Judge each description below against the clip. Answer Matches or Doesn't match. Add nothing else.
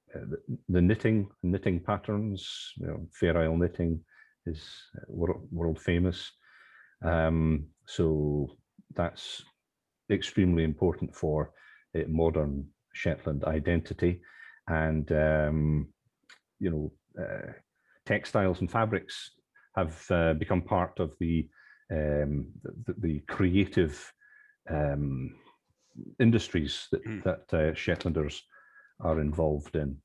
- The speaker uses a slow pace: Matches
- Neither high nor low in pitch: Doesn't match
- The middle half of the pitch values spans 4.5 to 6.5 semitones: Doesn't match